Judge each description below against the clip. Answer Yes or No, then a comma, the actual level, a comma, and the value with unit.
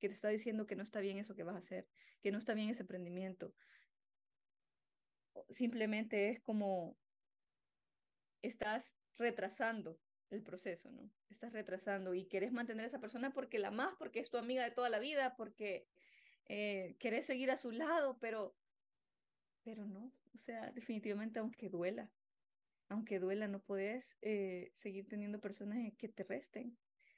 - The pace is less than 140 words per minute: No, average, 160 wpm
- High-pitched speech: Yes, high, 215 Hz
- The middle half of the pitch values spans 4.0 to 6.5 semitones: No, average, 3.2 semitones